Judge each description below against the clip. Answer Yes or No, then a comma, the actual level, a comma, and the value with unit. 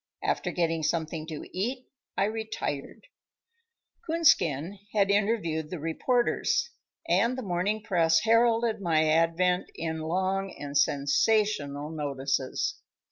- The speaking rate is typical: No, slow, 110 wpm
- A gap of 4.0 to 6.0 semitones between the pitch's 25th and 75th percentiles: Yes, wide, 5.5 semitones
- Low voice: No, medium, 175 Hz